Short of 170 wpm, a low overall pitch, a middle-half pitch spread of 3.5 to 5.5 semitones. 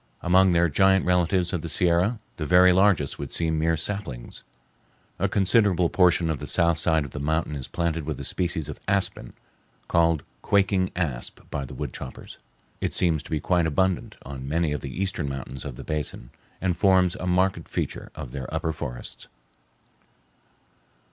No: average, 175 wpm; very low, 85 Hz; average, 3.8 semitones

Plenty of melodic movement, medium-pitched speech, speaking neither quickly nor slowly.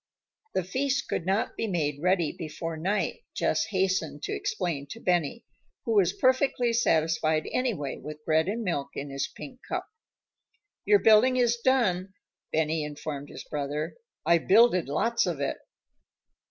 Yes: wide, 7.0 semitones; medium, 180 Hz; average, 150 wpm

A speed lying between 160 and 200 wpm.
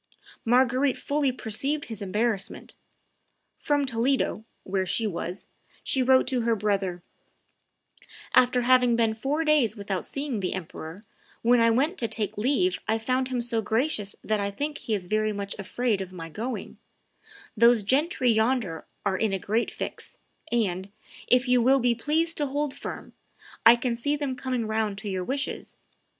Yes: average, 165 wpm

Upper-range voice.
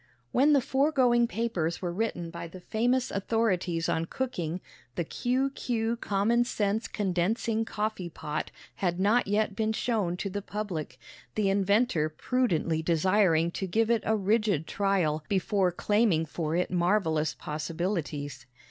Yes: high, 195 Hz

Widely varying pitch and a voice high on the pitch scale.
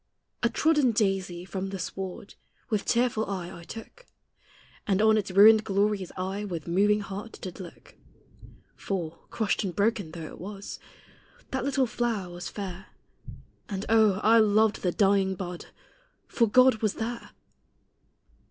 No: average, 2.8 semitones; high, 200 Hz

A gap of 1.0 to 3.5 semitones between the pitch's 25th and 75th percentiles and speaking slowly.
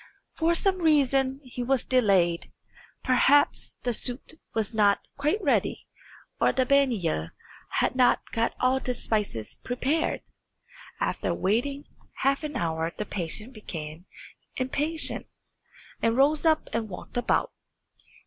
No: average, 5.0 semitones; slow, 125 wpm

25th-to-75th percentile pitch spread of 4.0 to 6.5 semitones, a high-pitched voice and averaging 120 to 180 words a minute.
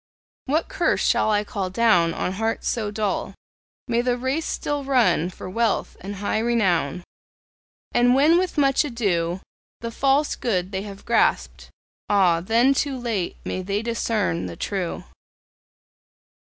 Yes: average, 4.7 semitones; high, 220 Hz; average, 150 wpm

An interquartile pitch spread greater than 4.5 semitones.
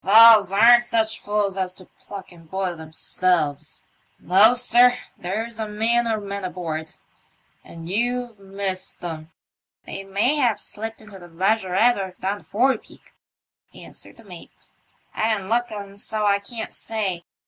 No: average, 3.3 semitones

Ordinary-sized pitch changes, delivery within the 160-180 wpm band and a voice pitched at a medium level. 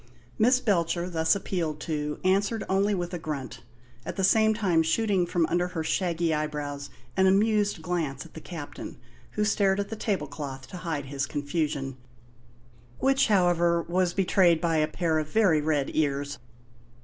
Yes: average, 4.1 semitones; average, 165 wpm; medium, 170 Hz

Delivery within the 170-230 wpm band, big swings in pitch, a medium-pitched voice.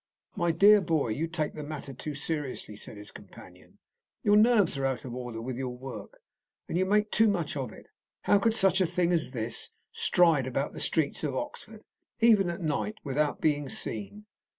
Yes: average, 195 wpm; wide, 6.7 semitones; medium, 155 Hz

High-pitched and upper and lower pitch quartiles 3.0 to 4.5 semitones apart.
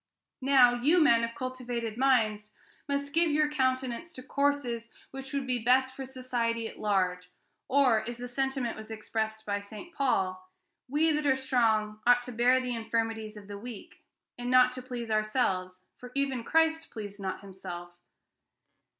Yes: high, 245 Hz; average, 3.5 semitones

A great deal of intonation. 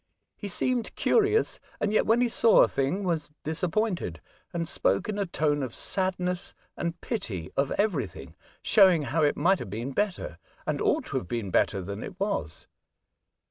Yes: wide, 7.3 semitones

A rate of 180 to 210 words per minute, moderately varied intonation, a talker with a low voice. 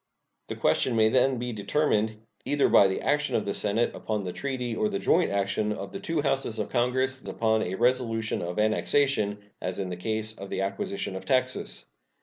Yes: average, 195 wpm; average, 4.1 semitones; low, 115 Hz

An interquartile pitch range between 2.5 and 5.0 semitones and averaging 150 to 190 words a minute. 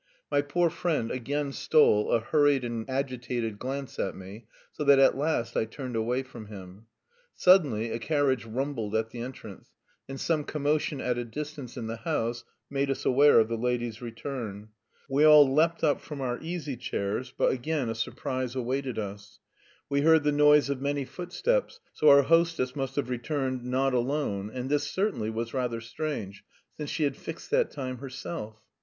Yes: average, 4.0 semitones; average, 180 wpm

